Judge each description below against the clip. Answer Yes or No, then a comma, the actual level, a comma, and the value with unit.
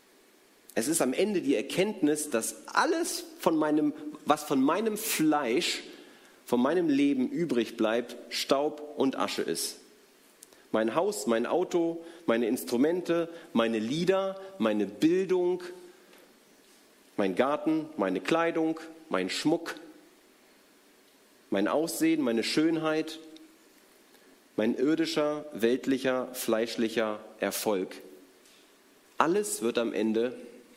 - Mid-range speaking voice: Yes, medium, 155 Hz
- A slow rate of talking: Yes, slow, 100 wpm